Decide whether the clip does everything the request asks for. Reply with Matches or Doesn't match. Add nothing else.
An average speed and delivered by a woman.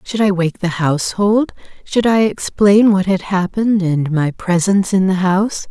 Matches